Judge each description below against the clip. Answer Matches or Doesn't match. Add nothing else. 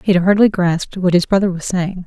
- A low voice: Doesn't match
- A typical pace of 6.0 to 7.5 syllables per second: Matches